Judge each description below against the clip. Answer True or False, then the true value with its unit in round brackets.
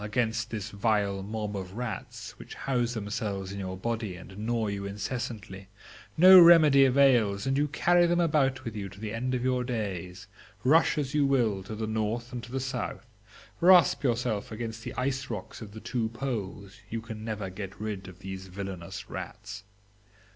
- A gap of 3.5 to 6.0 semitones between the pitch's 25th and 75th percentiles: True (4.3 semitones)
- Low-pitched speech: True (110 Hz)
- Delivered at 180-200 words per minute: True (185 wpm)